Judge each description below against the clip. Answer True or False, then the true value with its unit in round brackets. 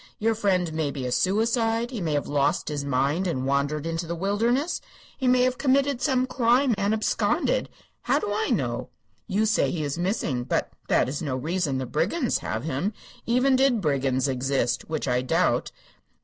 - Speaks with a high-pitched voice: False (180 Hz)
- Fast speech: False (185 wpm)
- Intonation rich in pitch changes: True (8.8 semitones)